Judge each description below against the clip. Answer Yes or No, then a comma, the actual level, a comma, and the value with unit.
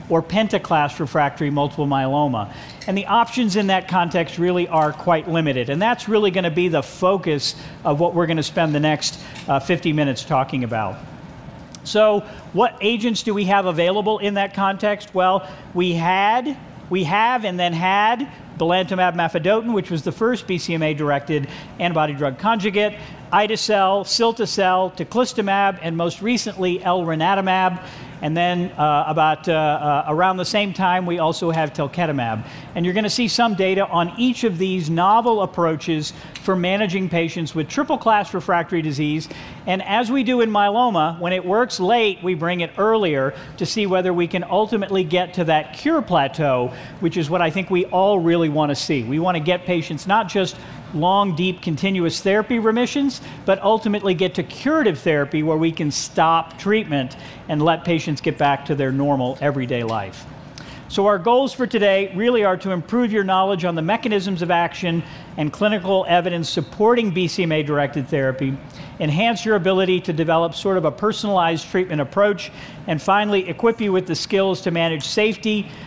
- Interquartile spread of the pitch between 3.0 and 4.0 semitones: No, average, 4.4 semitones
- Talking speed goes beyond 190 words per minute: No, average, 175 wpm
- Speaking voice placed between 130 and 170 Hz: No, medium, 180 Hz